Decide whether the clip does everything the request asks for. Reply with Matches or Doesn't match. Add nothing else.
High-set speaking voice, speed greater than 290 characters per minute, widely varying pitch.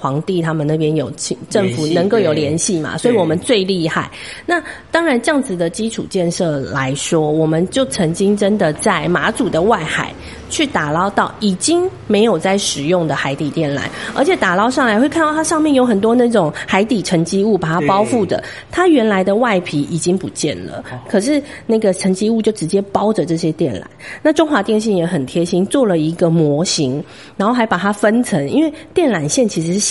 Matches